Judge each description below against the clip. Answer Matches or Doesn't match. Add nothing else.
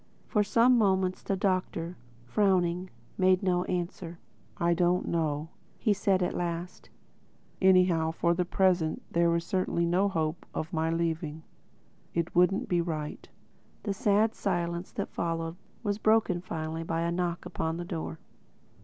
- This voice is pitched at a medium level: Matches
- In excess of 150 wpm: Doesn't match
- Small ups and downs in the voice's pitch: Matches